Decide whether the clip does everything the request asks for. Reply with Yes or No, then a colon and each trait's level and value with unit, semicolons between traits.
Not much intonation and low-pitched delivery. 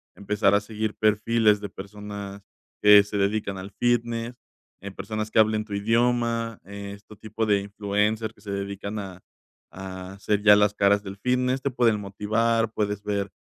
Yes: narrow, 1.7 semitones; low, 105 Hz